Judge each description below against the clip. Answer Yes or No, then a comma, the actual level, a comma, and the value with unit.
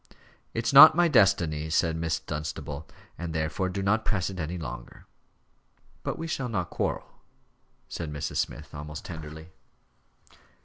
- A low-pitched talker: Yes, very low, 80 Hz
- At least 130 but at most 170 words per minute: Yes, average, 145 wpm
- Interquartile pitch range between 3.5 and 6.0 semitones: Yes, average, 4.3 semitones